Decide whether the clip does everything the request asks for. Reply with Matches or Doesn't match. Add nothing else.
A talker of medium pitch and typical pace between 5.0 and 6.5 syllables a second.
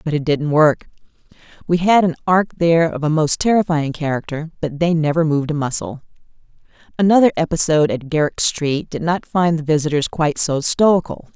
Matches